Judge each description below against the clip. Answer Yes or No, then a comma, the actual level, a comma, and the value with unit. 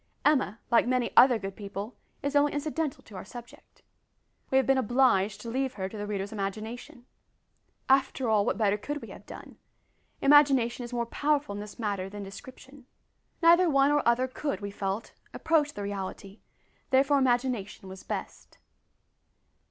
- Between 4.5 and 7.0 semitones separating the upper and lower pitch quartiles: Yes, average, 5.1 semitones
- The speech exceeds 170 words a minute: No, average, 165 wpm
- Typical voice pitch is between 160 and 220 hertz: No, high, 240 Hz